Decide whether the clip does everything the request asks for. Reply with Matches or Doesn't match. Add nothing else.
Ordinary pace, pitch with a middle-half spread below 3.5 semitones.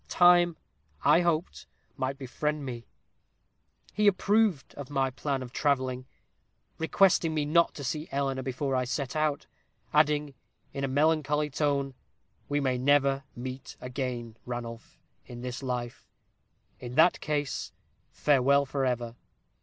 Doesn't match